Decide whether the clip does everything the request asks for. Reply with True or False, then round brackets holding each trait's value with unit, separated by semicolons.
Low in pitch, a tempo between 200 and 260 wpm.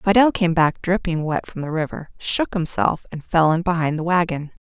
False (170 Hz; 205 wpm)